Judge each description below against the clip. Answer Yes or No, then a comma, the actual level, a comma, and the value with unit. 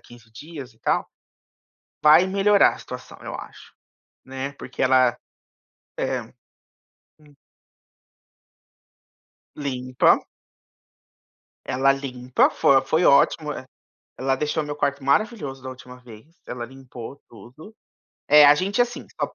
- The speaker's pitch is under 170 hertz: Yes, low, 135 Hz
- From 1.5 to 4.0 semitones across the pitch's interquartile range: Yes, average, 2.9 semitones